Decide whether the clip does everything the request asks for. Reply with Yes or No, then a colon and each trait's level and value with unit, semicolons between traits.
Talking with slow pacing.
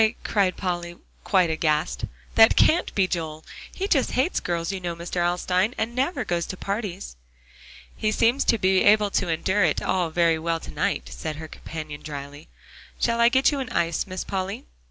No: average, 185 wpm